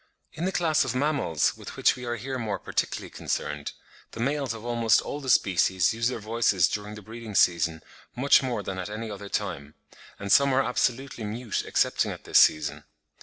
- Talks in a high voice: No, low, 115 Hz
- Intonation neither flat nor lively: Yes, average, 4.6 semitones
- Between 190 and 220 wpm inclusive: Yes, average, 195 wpm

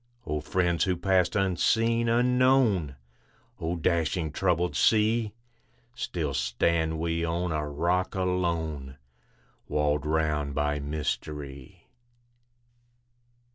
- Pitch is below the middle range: Yes, very low, 85 Hz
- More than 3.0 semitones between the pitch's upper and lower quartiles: Yes, average, 3.9 semitones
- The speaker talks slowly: Yes, slow, 95 wpm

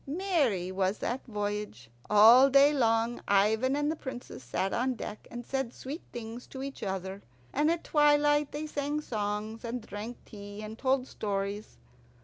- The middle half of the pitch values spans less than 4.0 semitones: No, average, 5.0 semitones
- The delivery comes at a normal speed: Yes, average, 160 wpm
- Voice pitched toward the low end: No, high, 235 Hz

